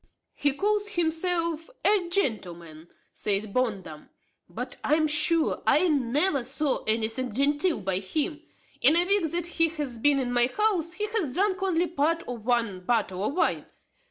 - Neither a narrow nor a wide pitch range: No, wide, 6.8 semitones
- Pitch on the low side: No, very high, 295 Hz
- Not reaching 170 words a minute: Yes, average, 160 wpm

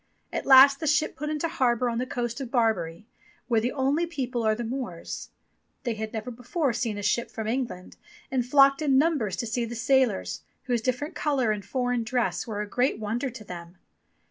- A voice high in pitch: Yes, high, 245 Hz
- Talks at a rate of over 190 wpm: Yes, average, 200 wpm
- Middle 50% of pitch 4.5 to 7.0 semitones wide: No, average, 3.5 semitones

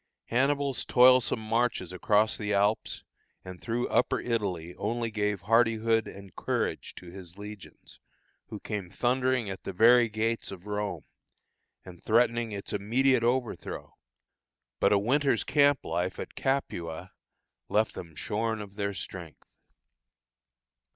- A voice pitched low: Yes, low, 110 Hz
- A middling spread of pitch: Yes, average, 3.4 semitones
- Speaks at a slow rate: Yes, slow, 130 wpm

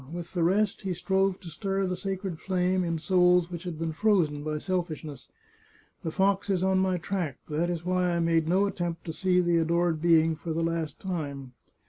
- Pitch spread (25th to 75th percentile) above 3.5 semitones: No, narrow, 2.4 semitones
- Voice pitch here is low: No, medium, 175 Hz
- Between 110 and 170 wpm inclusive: No, average, 200 wpm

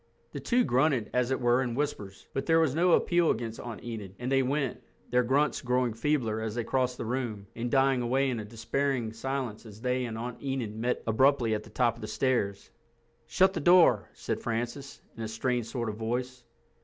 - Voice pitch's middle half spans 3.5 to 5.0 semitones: No, average, 3.0 semitones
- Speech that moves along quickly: Yes, fast, 210 wpm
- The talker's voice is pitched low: Yes, low, 125 Hz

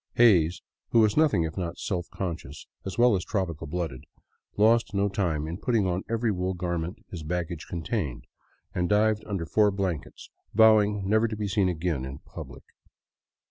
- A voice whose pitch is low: Yes, very low, 95 Hz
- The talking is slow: No, average, 170 wpm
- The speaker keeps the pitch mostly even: No, average, 4.0 semitones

